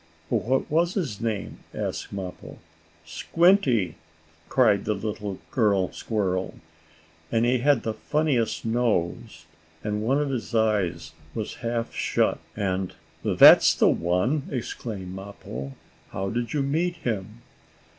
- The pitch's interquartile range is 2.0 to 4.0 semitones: No, average, 4.7 semitones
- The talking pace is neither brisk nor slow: No, slow, 125 wpm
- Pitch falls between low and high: No, low, 110 Hz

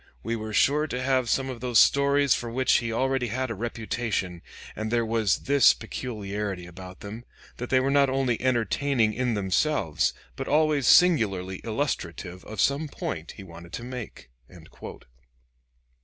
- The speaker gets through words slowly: No, average, 155 wpm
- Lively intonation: No, average, 4.6 semitones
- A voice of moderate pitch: No, low, 120 Hz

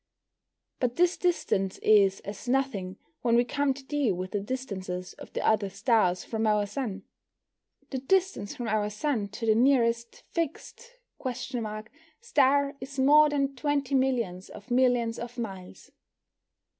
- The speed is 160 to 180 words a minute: No, average, 145 wpm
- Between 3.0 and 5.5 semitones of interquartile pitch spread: Yes, average, 5.1 semitones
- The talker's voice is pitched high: Yes, high, 240 Hz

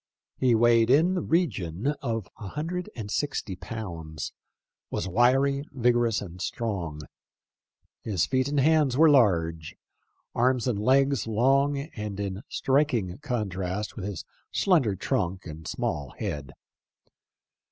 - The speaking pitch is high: No, low, 115 Hz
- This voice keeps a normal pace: No, slow, 125 wpm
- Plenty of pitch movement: Yes, wide, 6.6 semitones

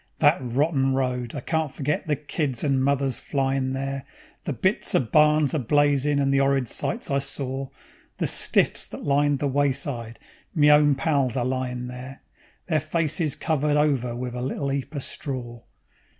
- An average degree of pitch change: No, narrow, 2.2 semitones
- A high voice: No, low, 135 Hz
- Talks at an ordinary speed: Yes, average, 170 wpm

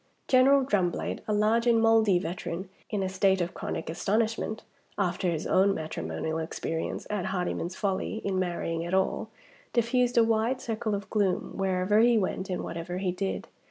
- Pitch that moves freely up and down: No, average, 3.8 semitones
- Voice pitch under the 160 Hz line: No, high, 195 Hz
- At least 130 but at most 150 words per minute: No, average, 165 wpm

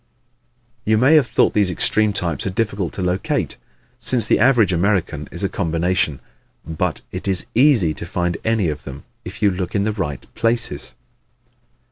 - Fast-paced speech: No, average, 170 wpm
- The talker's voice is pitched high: No, very low, 95 Hz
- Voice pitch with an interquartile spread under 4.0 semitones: No, average, 4.3 semitones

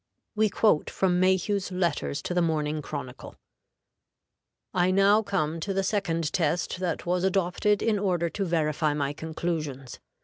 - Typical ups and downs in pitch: Yes, average, 3.9 semitones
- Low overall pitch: No, medium, 175 Hz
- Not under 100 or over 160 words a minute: Yes, average, 145 wpm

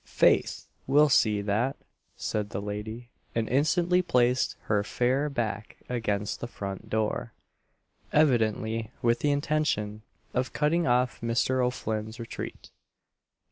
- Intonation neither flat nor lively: Yes, average, 4.0 semitones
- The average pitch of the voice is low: Yes, low, 120 Hz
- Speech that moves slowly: Yes, slow, 120 wpm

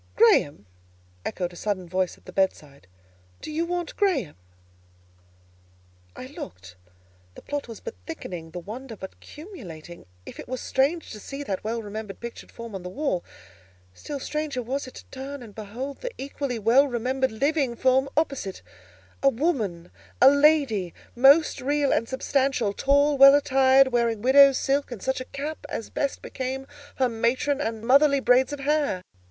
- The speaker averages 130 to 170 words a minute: Yes, average, 160 wpm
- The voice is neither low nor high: No, very high, 260 Hz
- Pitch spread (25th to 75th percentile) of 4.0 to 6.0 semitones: Yes, average, 4.8 semitones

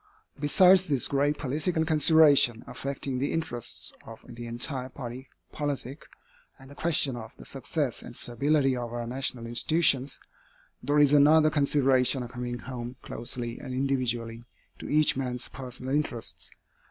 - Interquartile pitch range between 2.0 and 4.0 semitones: Yes, average, 3.3 semitones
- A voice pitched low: Yes, low, 130 Hz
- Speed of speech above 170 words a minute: No, average, 140 wpm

